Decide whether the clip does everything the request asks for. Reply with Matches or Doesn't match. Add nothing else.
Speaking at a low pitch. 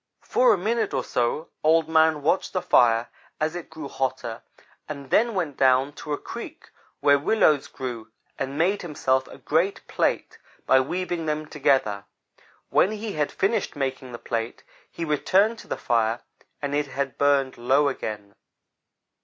Doesn't match